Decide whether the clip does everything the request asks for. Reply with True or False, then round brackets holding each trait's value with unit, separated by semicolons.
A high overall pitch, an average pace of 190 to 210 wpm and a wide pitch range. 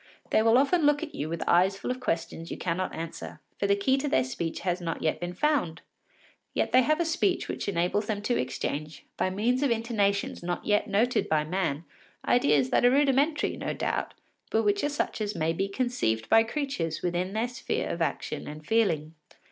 True (200 Hz; 205 wpm; 7.0 semitones)